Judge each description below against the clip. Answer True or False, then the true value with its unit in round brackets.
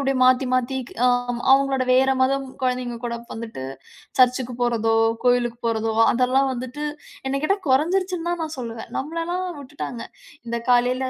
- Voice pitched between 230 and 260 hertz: True (255 Hz)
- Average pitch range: False (2.2 semitones)